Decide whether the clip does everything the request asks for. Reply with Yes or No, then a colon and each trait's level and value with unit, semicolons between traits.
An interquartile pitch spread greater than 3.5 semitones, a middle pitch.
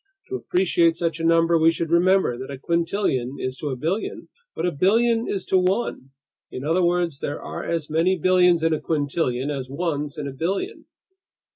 Yes: average, 4.0 semitones; medium, 165 Hz